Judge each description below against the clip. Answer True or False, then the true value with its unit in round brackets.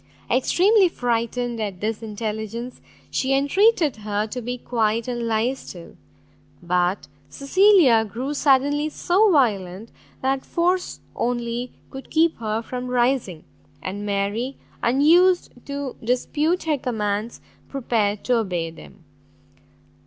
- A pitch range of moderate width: True (4.7 semitones)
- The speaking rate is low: True (115 wpm)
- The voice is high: True (245 Hz)